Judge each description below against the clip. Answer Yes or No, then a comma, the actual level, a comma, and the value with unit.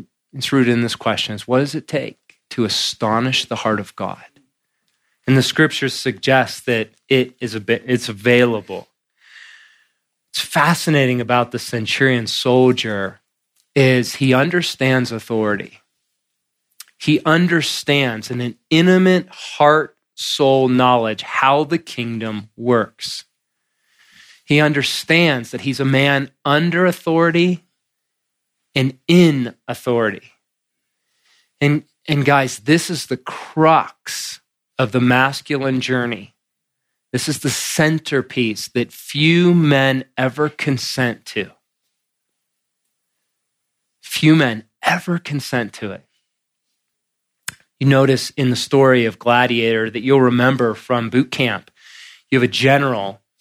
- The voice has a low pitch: Yes, low, 130 Hz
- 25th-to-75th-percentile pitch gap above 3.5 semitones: No, average, 3.2 semitones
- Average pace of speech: No, slow, 115 wpm